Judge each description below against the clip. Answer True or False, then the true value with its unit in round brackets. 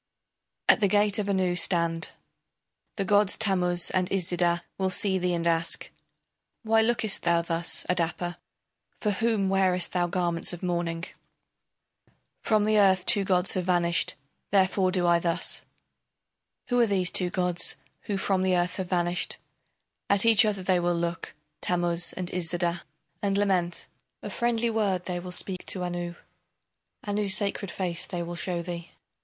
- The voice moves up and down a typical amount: False (2.3 semitones)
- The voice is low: False (180 Hz)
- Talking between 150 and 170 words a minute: True (160 wpm)